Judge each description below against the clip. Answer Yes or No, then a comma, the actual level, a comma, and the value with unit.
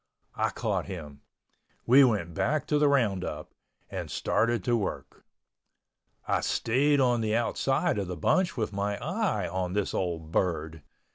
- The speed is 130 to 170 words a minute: Yes, average, 150 wpm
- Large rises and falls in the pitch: Yes, wide, 6.5 semitones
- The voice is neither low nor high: No, low, 105 Hz